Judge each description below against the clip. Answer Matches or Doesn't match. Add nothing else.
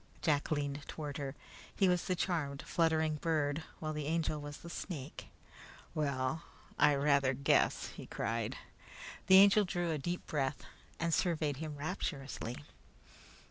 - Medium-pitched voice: Matches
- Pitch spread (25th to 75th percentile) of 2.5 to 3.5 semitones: Matches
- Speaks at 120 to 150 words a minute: Matches